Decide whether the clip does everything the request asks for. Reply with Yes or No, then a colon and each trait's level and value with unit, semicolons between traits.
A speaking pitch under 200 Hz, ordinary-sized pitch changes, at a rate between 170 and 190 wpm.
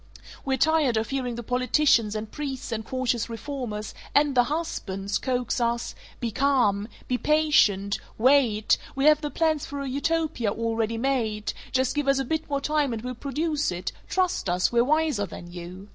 No: very high, 255 Hz; average, 4.8 semitones; average, 175 wpm